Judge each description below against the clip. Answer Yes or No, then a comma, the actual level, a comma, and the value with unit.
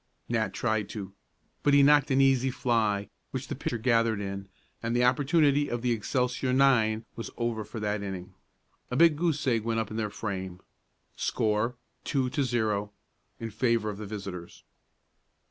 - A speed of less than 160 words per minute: No, average, 165 wpm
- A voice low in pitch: Yes, low, 115 Hz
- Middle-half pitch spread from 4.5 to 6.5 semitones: No, average, 3.5 semitones